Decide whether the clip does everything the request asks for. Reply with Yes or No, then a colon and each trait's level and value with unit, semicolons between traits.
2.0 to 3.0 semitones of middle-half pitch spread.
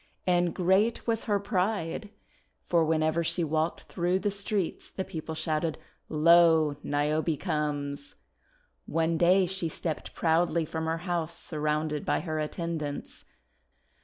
Yes: narrow, 2.5 semitones